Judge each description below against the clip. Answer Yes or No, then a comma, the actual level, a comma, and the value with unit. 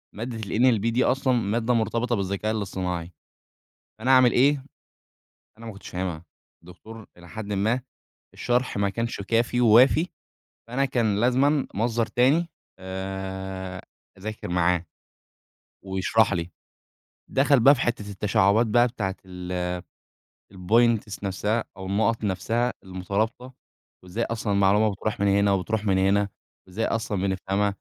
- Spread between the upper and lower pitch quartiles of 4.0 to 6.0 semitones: No, average, 3.6 semitones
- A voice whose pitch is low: Yes, low, 105 Hz